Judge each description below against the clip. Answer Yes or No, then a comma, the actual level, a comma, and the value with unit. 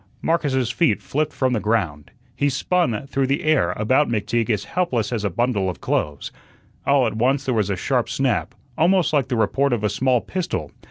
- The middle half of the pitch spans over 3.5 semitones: Yes, average, 4.8 semitones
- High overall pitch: No, low, 125 Hz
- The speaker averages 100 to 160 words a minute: No, average, 200 wpm